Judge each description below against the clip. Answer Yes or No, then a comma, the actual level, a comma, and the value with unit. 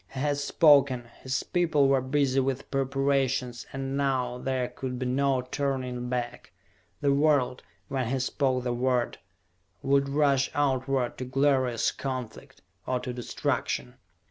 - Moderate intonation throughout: No, narrow, 1.6 semitones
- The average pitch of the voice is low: Yes, low, 130 Hz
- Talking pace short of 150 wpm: Yes, average, 140 wpm